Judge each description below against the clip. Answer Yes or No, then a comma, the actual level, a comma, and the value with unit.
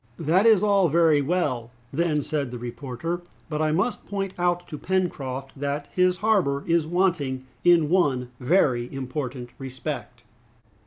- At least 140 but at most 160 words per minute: Yes, average, 145 wpm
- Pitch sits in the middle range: Yes, medium, 155 Hz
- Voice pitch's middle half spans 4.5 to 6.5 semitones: Yes, average, 5.1 semitones